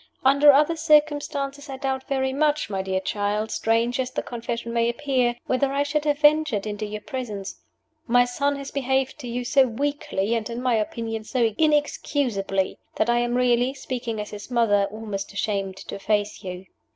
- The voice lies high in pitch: Yes, high, 245 Hz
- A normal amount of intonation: Yes, average, 4.5 semitones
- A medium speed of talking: Yes, average, 180 wpm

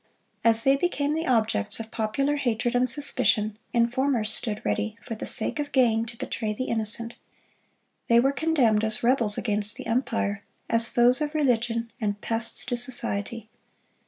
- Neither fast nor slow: Yes, average, 160 wpm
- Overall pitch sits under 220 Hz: No, high, 235 Hz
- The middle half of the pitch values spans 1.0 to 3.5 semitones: Yes, average, 2.9 semitones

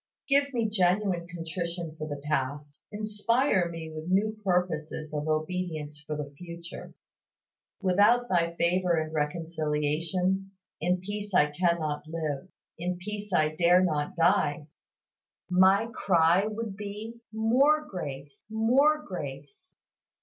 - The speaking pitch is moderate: Yes, medium, 175 Hz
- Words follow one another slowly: Yes, slow, 120 wpm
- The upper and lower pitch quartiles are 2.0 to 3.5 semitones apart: No, average, 4.8 semitones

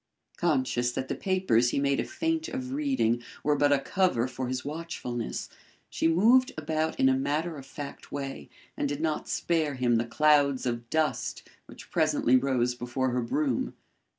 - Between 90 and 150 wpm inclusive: No, average, 175 wpm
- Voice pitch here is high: No, medium, 140 Hz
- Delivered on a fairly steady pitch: No, average, 4.5 semitones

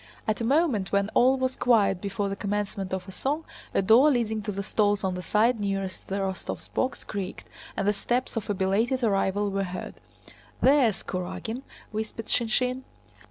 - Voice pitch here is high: Yes, high, 210 Hz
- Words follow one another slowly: No, average, 180 wpm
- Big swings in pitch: No, average, 3.7 semitones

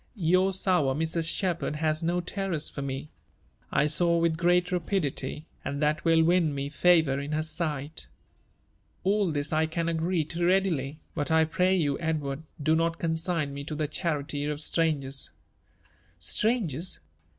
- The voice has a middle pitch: Yes, medium, 160 Hz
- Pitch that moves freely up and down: No, average, 2.8 semitones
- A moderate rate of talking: Yes, average, 165 wpm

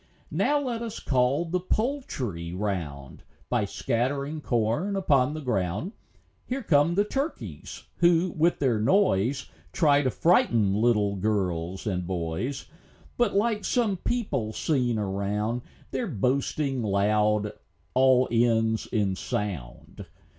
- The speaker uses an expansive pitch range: Yes, wide, 8.4 semitones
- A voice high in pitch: No, low, 125 Hz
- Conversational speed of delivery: No, slow, 120 wpm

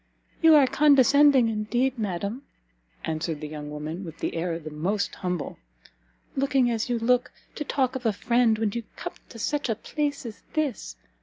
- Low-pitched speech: No, high, 230 Hz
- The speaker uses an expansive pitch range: Yes, wide, 6.8 semitones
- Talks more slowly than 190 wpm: Yes, average, 175 wpm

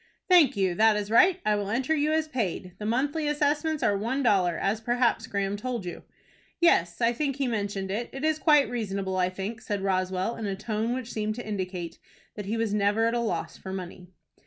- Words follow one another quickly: Yes, fast, 215 wpm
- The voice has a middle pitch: No, high, 215 Hz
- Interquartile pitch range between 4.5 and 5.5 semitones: Yes, average, 4.8 semitones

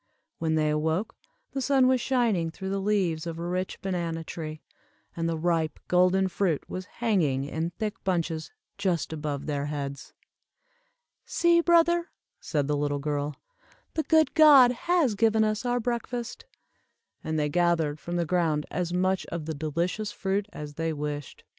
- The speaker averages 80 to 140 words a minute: No, average, 160 wpm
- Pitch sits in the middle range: Yes, medium, 175 Hz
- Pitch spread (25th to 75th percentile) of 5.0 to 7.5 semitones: Yes, wide, 5.6 semitones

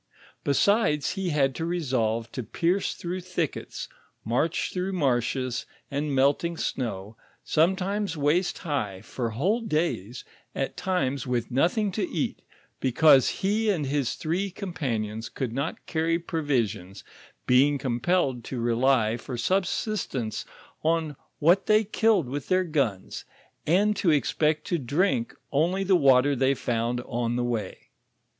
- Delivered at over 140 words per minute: No, slow, 135 wpm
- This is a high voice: No, medium, 145 Hz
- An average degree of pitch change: No, wide, 6.5 semitones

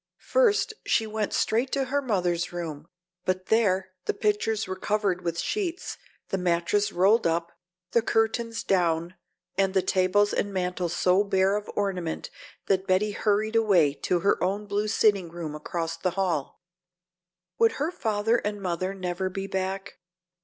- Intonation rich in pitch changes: No, average, 3.0 semitones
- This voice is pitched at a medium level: No, high, 195 Hz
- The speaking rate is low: No, average, 155 wpm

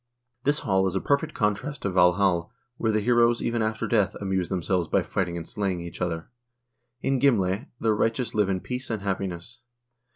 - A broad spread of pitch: No, average, 4.3 semitones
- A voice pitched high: No, low, 100 Hz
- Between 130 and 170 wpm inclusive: No, average, 185 wpm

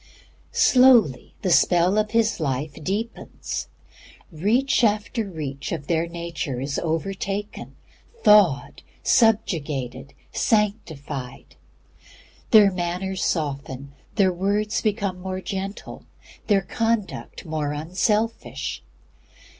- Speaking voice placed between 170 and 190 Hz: Yes, medium, 185 Hz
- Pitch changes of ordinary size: No, wide, 5.7 semitones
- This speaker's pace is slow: Yes, slow, 90 wpm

